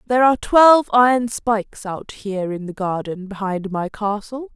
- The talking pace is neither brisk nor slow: Yes, average, 170 wpm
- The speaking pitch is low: No, high, 215 Hz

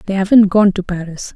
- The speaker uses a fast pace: Yes, fast, 220 wpm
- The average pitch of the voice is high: Yes, high, 195 Hz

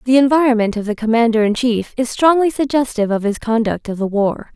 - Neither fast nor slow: No, fast, 210 wpm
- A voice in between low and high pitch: No, high, 235 Hz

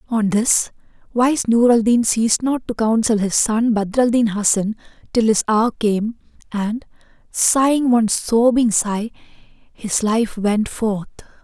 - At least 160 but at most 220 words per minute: No, average, 150 wpm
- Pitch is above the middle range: Yes, high, 225 Hz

